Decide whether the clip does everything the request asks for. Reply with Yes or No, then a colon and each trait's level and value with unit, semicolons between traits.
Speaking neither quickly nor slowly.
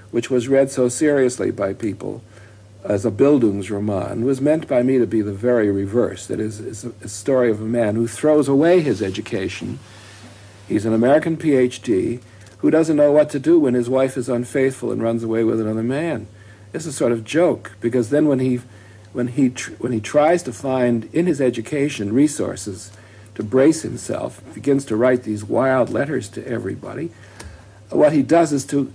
Yes: average, 190 wpm